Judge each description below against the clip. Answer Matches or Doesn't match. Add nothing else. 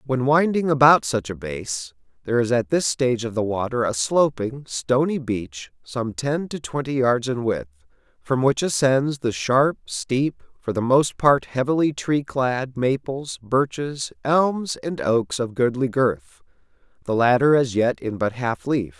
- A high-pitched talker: Doesn't match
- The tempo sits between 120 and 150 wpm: Doesn't match